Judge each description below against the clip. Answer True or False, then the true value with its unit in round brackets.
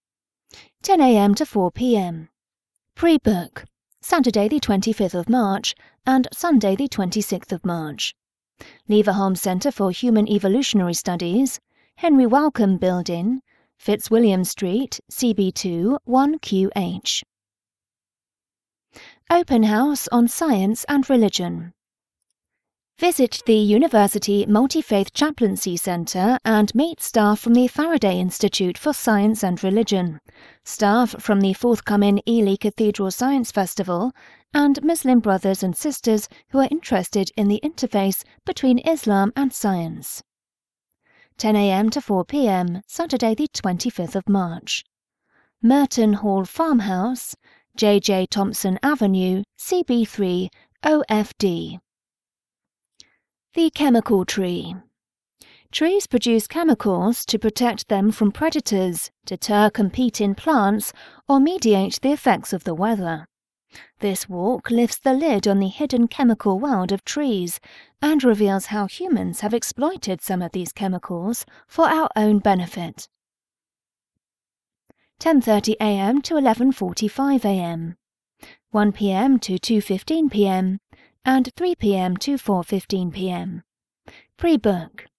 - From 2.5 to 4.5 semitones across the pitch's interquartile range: False (5.1 semitones)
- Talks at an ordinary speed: False (110 wpm)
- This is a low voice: False (210 Hz)